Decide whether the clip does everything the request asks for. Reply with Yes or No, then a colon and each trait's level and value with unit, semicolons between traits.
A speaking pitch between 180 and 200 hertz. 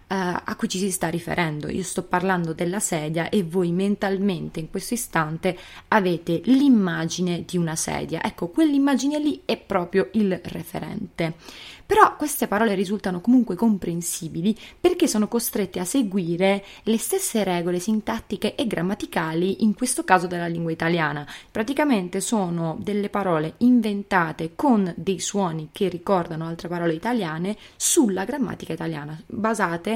Yes: high, 190 Hz